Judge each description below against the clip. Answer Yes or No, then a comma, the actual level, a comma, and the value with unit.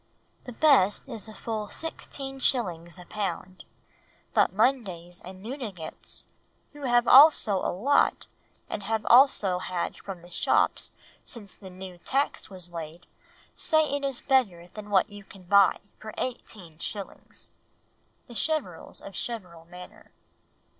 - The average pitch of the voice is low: No, high, 205 Hz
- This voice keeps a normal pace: No, slow, 130 wpm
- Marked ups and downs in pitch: Yes, wide, 5.7 semitones